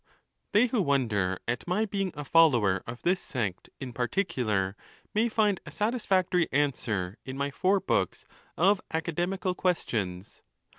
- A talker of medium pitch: Yes, medium, 150 Hz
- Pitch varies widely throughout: Yes, wide, 9.0 semitones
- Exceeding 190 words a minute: No, average, 140 wpm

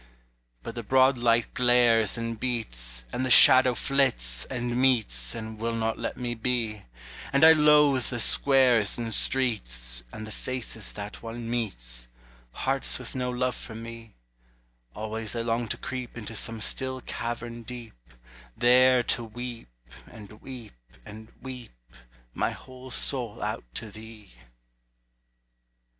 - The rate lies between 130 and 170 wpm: Yes, average, 140 wpm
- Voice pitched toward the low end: Yes, low, 115 Hz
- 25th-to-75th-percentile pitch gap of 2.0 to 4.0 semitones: Yes, average, 2.7 semitones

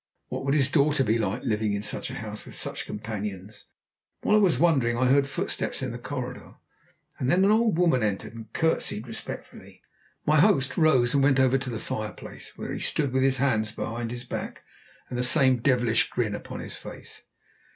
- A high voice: No, low, 125 Hz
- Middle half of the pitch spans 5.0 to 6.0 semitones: No, average, 3.8 semitones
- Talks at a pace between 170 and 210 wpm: Yes, average, 200 wpm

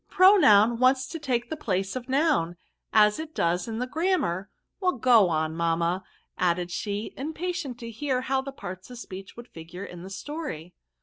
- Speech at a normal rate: Yes, average, 180 wpm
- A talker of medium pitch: No, high, 230 Hz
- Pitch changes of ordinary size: No, wide, 7.1 semitones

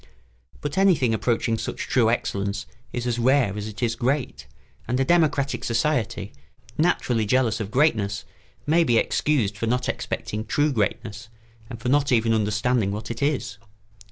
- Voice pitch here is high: No, low, 120 Hz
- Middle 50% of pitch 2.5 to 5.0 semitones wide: Yes, average, 4.1 semitones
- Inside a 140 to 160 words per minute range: Yes, average, 155 wpm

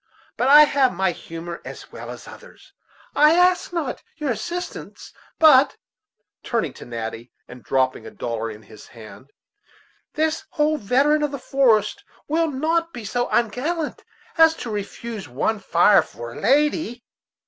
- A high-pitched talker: Yes, high, 245 Hz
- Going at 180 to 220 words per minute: No, average, 150 wpm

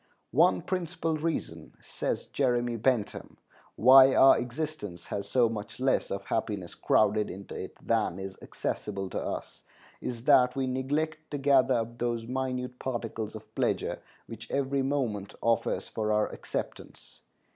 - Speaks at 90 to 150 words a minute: Yes, average, 145 wpm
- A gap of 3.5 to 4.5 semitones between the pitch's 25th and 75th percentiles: Yes, average, 3.9 semitones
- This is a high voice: No, low, 120 Hz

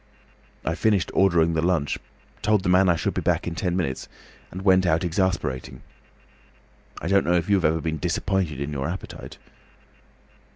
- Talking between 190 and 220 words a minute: No, average, 175 wpm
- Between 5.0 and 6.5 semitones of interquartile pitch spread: No, average, 2.9 semitones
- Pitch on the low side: Yes, very low, 85 Hz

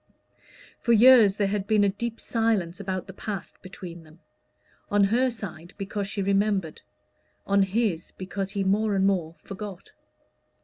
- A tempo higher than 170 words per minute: No, average, 150 wpm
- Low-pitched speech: No, high, 200 Hz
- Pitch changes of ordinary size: No, narrow, 2.1 semitones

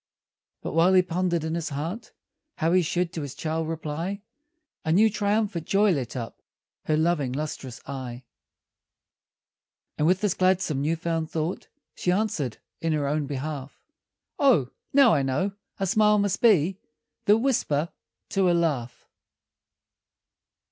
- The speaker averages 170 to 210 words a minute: No, average, 145 wpm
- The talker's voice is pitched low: No, medium, 165 Hz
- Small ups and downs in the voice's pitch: No, average, 4.4 semitones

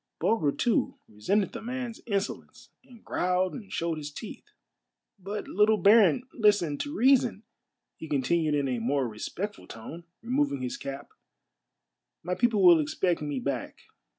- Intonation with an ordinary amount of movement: No, wide, 7.2 semitones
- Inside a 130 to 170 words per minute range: Yes, average, 150 wpm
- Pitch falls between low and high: Yes, medium, 180 Hz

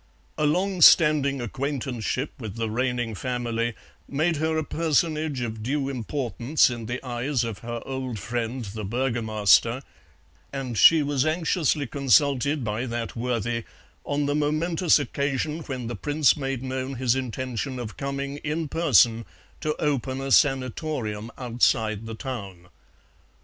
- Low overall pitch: Yes, low, 130 Hz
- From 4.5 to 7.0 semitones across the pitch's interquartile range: No, average, 3.8 semitones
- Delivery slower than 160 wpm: Yes, average, 140 wpm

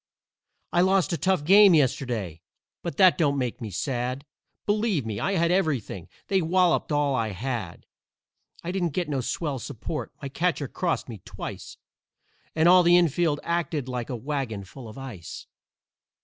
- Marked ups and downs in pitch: Yes, wide, 6.1 semitones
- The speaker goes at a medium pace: Yes, average, 165 wpm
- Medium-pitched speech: Yes, medium, 145 Hz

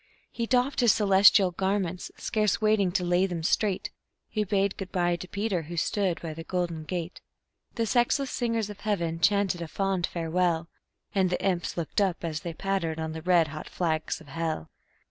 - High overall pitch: No, medium, 180 Hz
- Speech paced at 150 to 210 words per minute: Yes, average, 185 wpm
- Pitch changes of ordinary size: Yes, average, 3.3 semitones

